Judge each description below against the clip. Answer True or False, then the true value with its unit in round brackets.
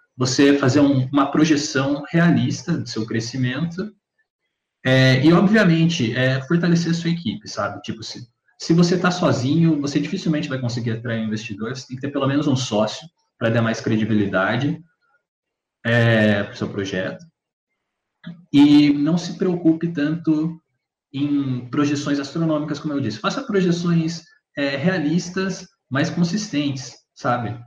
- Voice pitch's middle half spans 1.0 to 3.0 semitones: False (5.2 semitones)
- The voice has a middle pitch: True (145 Hz)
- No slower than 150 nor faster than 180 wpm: False (140 wpm)